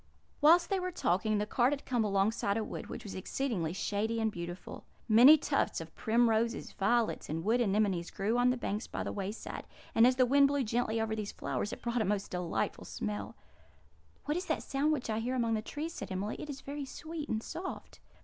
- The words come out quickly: Yes, fast, 215 wpm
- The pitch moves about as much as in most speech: Yes, average, 4.5 semitones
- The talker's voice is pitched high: Yes, high, 225 Hz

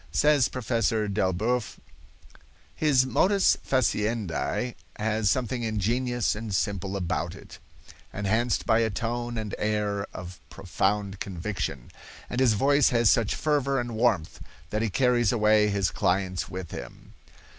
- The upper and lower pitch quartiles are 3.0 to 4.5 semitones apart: Yes, average, 3.6 semitones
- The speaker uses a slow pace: Yes, slow, 130 wpm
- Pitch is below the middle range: Yes, low, 110 Hz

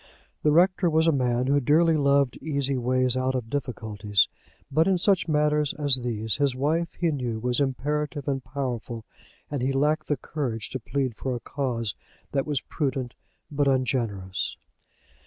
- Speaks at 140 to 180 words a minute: Yes, average, 165 wpm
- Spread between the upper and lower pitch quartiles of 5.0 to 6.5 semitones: No, average, 3.2 semitones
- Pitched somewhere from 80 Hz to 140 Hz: Yes, low, 135 Hz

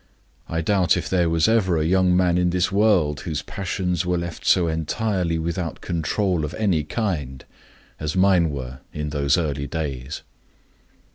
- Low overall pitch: Yes, very low, 85 Hz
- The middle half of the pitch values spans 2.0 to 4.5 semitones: Yes, average, 3.3 semitones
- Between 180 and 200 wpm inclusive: No, average, 160 wpm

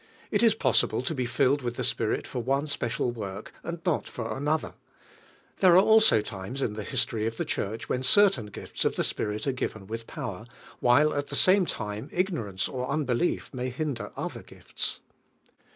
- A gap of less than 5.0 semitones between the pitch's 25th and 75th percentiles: No, wide, 5.5 semitones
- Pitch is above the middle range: No, low, 125 Hz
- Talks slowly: No, average, 185 wpm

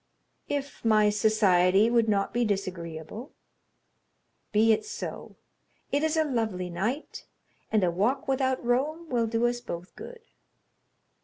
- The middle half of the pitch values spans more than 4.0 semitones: Yes, average, 5.0 semitones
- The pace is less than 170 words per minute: Yes, slow, 135 wpm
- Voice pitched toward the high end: Yes, high, 225 Hz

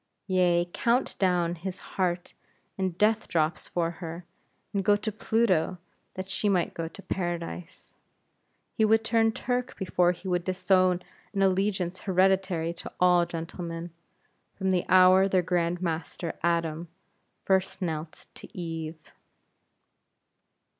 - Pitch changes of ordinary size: No, narrow, 2.2 semitones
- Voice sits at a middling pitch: Yes, medium, 180 Hz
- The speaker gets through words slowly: Yes, slow, 130 wpm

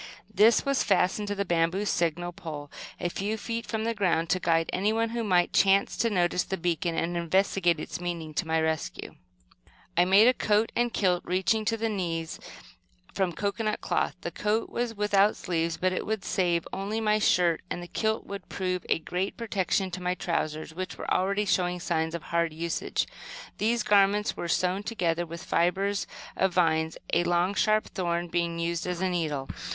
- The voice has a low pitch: No, medium, 185 Hz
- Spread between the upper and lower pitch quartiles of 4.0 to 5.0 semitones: No, average, 3.4 semitones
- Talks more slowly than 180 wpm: No, average, 190 wpm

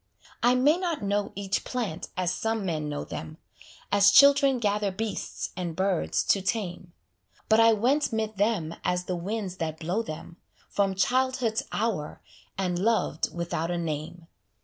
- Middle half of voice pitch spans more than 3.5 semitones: Yes, average, 4.5 semitones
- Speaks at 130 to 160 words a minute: Yes, average, 155 wpm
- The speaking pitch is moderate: No, high, 200 Hz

